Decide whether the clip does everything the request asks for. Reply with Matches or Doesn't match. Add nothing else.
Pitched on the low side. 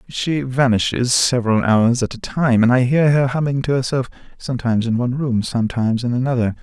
Matches